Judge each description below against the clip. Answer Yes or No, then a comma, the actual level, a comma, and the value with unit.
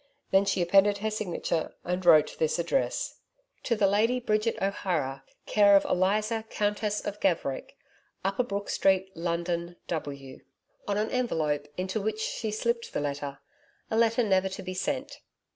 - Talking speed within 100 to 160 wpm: Yes, average, 155 wpm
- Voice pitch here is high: Yes, high, 195 Hz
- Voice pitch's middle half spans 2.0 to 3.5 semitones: No, average, 4.0 semitones